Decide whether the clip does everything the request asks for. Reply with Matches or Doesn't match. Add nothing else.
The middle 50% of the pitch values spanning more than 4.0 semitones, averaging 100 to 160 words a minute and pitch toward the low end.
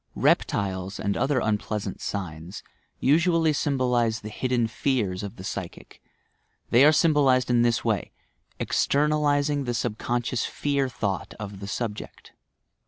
Matches